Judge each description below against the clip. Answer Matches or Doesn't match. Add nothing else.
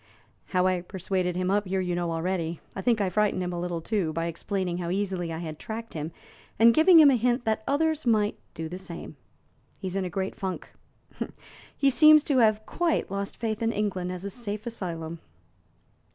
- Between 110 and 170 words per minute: Doesn't match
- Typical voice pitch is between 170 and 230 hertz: Matches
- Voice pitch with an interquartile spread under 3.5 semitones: Doesn't match